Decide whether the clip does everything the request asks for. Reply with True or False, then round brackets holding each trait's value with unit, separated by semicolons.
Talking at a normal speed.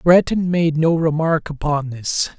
True (150 wpm)